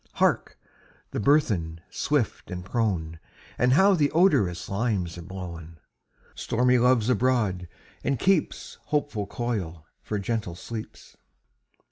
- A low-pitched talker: Yes, low, 110 Hz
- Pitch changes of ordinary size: No, wide, 6.1 semitones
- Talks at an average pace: No, slow, 115 wpm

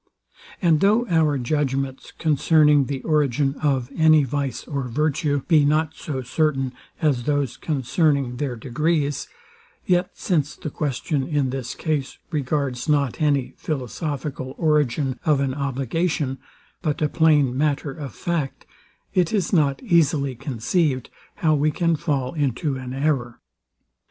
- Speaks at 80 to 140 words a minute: Yes, slow, 135 wpm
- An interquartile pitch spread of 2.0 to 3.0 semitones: Yes, average, 2.7 semitones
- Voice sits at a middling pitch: Yes, medium, 145 Hz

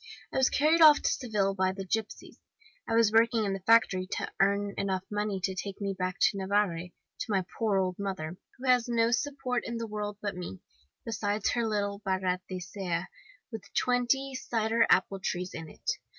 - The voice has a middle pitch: No, high, 205 Hz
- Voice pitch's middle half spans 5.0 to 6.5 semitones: No, average, 3.4 semitones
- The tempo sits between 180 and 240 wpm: Yes, average, 185 wpm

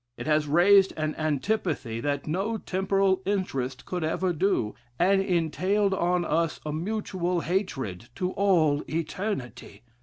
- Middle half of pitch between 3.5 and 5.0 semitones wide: Yes, average, 4.1 semitones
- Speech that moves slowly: Yes, slow, 130 wpm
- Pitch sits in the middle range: Yes, medium, 175 Hz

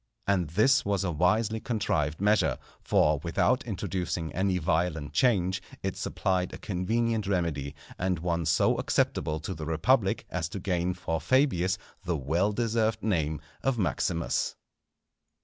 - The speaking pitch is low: Yes, very low, 90 Hz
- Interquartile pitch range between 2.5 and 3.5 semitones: No, average, 4.3 semitones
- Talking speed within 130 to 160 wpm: Yes, average, 140 wpm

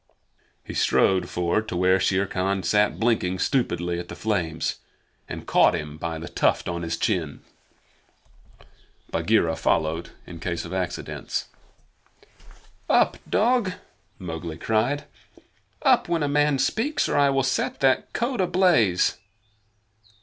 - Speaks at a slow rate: Yes, slow, 130 wpm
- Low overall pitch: Yes, very low, 95 Hz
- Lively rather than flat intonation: Yes, wide, 8.2 semitones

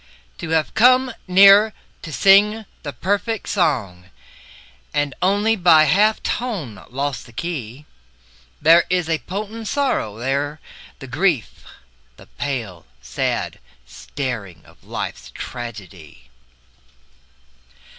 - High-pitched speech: No, medium, 155 Hz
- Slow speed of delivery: Yes, slow, 110 wpm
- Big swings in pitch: Yes, wide, 8.8 semitones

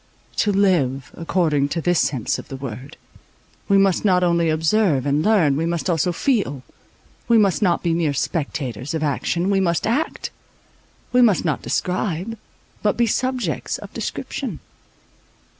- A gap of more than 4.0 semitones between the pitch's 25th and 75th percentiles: Yes, average, 5.2 semitones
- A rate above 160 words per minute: No, average, 155 wpm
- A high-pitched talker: No, medium, 170 Hz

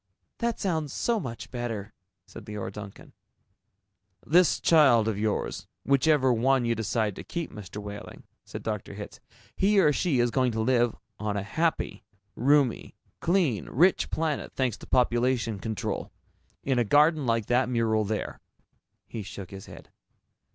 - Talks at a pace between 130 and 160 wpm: Yes, average, 150 wpm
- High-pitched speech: No, low, 120 Hz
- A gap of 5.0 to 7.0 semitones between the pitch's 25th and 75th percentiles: Yes, wide, 5.6 semitones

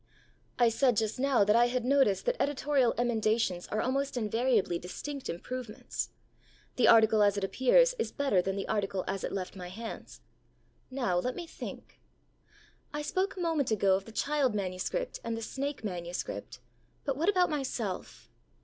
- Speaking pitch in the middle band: No, high, 235 Hz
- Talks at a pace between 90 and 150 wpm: No, average, 165 wpm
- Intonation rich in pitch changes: Yes, wide, 5.7 semitones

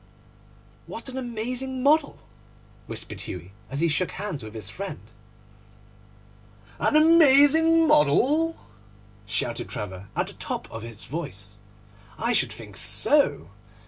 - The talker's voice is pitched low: No, high, 220 Hz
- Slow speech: Yes, slow, 120 wpm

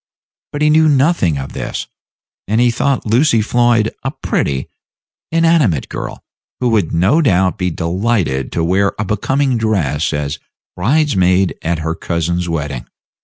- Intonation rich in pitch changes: Yes, wide, 7.2 semitones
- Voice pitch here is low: Yes, low, 100 Hz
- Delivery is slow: No, average, 145 wpm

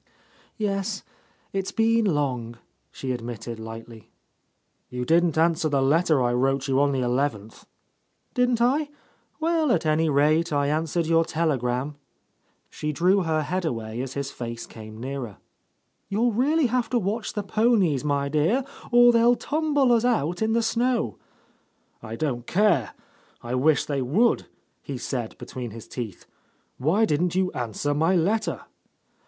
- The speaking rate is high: No, average, 150 wpm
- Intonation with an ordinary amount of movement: No, wide, 8.9 semitones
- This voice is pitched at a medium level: Yes, medium, 155 Hz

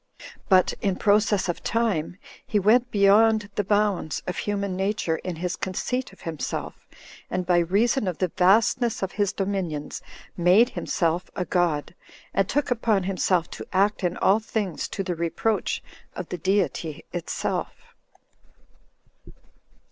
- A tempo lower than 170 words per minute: Yes, average, 140 wpm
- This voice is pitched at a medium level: No, high, 195 Hz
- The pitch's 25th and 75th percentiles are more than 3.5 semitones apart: No, average, 3.0 semitones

